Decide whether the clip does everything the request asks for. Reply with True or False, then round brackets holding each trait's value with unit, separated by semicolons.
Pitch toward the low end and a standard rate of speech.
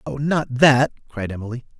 True (130 Hz; 165 wpm)